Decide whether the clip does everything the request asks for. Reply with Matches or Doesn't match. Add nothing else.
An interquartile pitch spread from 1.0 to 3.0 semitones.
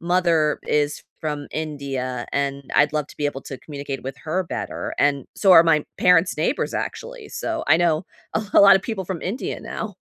Doesn't match